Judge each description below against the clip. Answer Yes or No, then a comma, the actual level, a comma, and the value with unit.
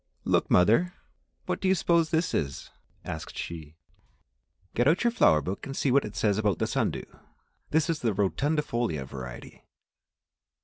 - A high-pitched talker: No, low, 115 Hz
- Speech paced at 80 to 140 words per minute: No, average, 165 wpm